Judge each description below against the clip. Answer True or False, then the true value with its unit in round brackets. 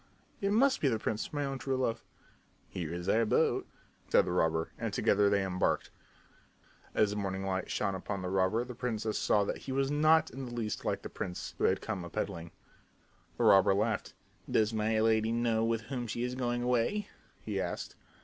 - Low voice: True (110 Hz)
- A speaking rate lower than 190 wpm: False (200 wpm)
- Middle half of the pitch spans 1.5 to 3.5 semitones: False (4.3 semitones)